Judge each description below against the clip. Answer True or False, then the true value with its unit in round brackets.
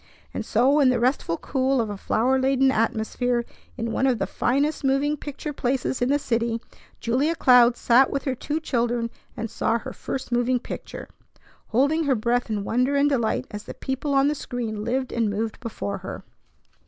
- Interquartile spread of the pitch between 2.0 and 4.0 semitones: True (2.7 semitones)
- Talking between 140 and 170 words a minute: False (190 wpm)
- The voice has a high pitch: True (250 Hz)